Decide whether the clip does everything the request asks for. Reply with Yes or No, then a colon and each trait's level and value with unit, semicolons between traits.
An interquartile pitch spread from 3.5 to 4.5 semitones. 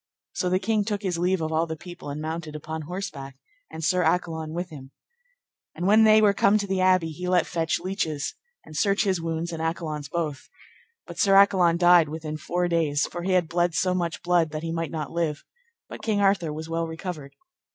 No: narrow, 2.6 semitones